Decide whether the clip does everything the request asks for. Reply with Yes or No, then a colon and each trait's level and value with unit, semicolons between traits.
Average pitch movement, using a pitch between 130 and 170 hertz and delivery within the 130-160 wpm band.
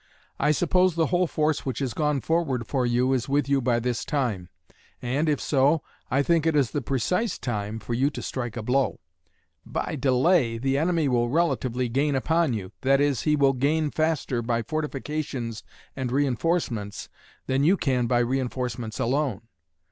No: average, 3.9 semitones; low, 135 Hz; average, 175 wpm